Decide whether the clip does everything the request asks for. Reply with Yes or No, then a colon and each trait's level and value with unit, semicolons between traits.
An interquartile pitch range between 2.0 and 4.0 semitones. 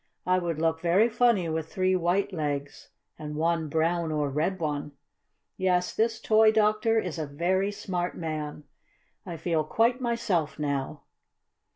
No: average, 4.4 semitones